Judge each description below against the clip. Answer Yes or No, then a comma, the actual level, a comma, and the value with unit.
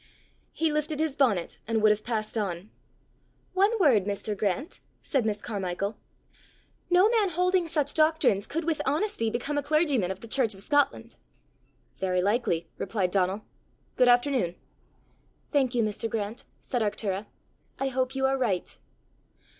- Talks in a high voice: Yes, high, 240 Hz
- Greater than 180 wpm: No, average, 155 wpm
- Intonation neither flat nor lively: No, wide, 6.3 semitones